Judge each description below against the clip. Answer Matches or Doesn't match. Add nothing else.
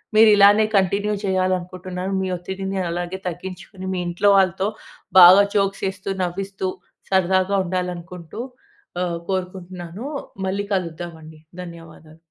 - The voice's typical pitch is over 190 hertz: Doesn't match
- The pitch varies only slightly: Matches